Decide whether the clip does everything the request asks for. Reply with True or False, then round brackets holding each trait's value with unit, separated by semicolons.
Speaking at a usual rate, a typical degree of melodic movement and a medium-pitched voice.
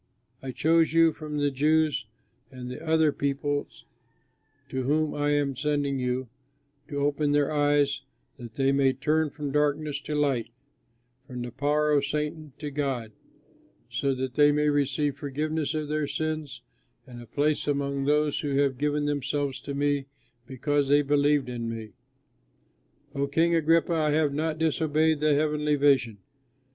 False (155 wpm; 1.7 semitones; 145 Hz)